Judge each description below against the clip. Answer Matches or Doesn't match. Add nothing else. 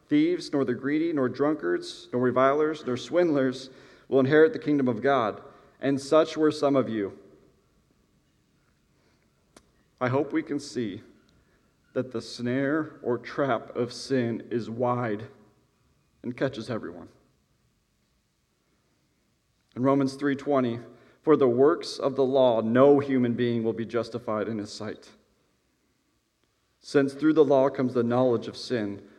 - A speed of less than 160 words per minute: Matches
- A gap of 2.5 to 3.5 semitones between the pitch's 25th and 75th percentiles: Matches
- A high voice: Doesn't match